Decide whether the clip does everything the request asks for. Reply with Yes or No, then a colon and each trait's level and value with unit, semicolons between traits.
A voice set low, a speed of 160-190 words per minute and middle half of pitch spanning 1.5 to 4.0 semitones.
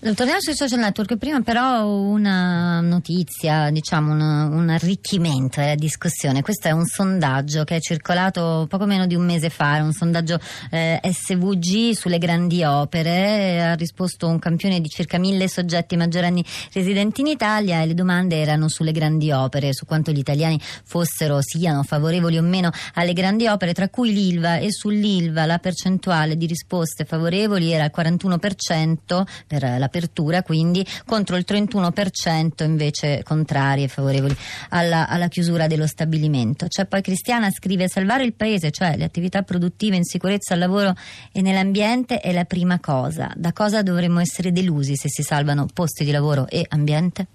No: medium, 175 Hz; average, 165 wpm; average, 3.3 semitones